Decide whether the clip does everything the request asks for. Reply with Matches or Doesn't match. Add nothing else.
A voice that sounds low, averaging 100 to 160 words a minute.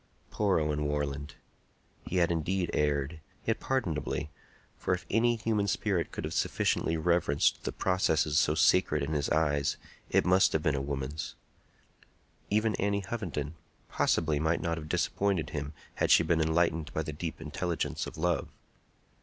Matches